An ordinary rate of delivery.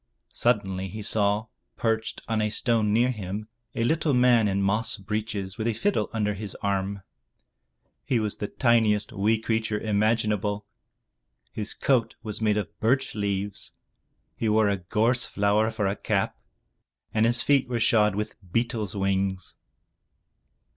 Yes: average, 145 wpm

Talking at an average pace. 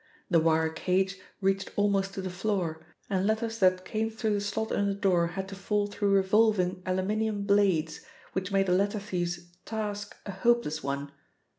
Yes: average, 175 wpm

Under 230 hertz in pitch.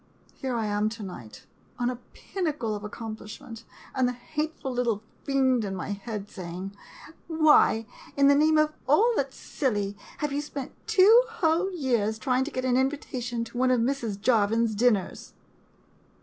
No: high, 245 Hz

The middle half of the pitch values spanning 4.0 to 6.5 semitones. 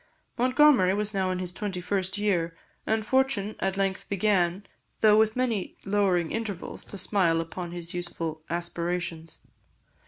No: average, 3.3 semitones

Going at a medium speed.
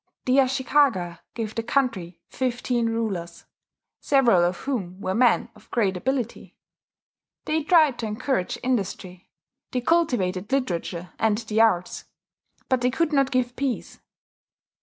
No: slow, 130 wpm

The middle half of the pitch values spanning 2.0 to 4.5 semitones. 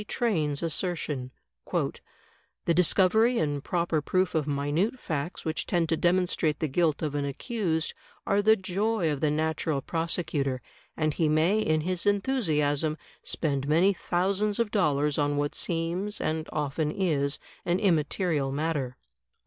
Yes: average, 3.9 semitones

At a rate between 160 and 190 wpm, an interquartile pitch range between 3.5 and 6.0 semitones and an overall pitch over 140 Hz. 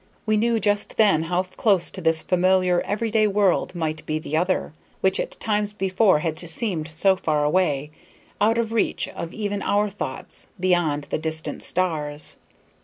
Yes: average, 170 wpm; average, 4.5 semitones; medium, 185 Hz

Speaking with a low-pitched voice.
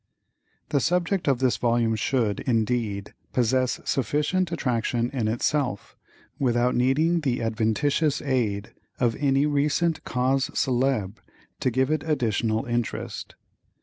Yes: low, 125 Hz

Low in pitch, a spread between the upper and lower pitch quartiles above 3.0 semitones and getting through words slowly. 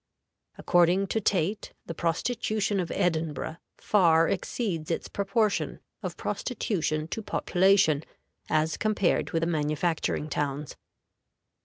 No: medium, 170 Hz; average, 4.1 semitones; slow, 110 wpm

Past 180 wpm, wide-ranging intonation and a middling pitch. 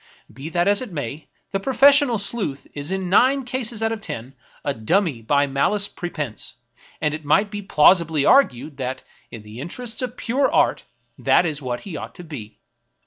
Yes: average, 190 wpm; wide, 7.7 semitones; medium, 170 Hz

